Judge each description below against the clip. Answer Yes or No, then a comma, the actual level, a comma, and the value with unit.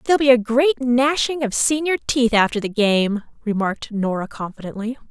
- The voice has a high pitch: Yes, high, 240 Hz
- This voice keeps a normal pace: Yes, average, 165 wpm